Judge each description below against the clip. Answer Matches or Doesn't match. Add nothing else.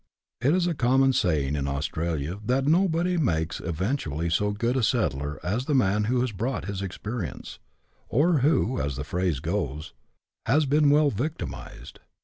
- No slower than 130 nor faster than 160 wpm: Doesn't match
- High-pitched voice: Doesn't match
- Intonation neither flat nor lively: Doesn't match